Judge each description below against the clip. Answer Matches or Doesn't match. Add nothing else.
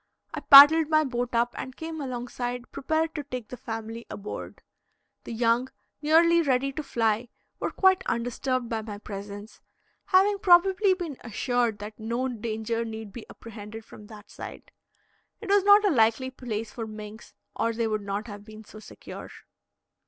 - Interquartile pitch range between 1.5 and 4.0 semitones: Doesn't match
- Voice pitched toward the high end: Matches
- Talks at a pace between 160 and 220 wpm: Matches